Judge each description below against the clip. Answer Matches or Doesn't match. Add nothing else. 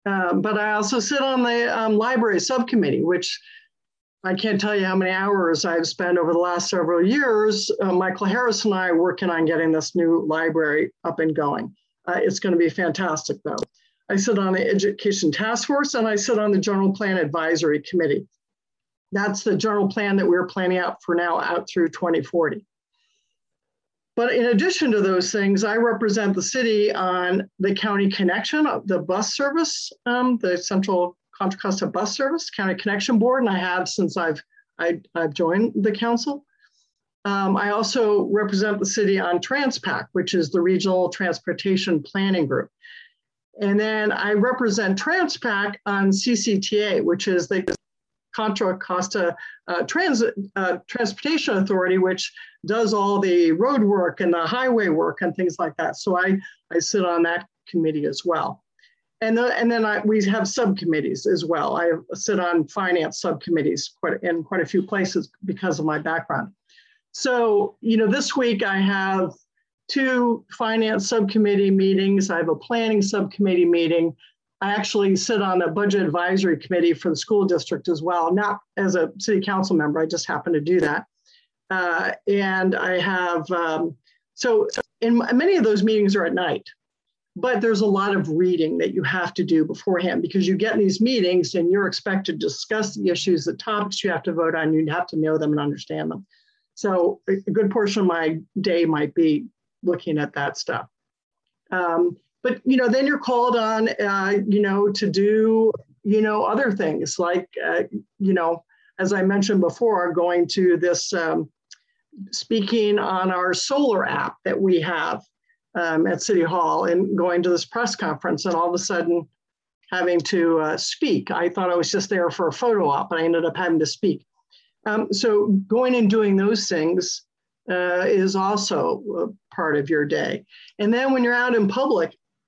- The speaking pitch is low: Doesn't match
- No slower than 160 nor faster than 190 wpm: Matches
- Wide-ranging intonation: Doesn't match